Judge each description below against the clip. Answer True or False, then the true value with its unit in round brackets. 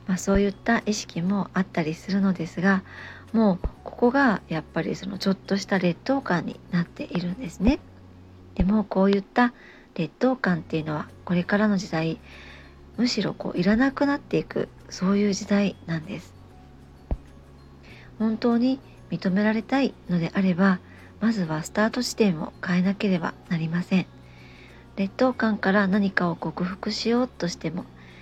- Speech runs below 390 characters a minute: True (320 characters per minute)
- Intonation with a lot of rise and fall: False (4.7 semitones)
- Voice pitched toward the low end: False (190 Hz)